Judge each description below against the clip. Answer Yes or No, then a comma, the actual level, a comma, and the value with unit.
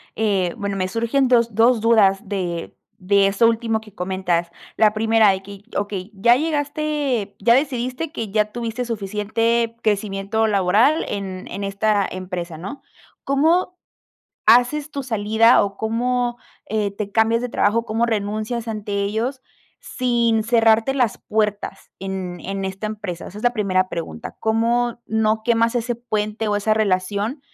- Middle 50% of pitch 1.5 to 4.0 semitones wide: Yes, average, 2.9 semitones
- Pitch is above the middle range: Yes, high, 220 Hz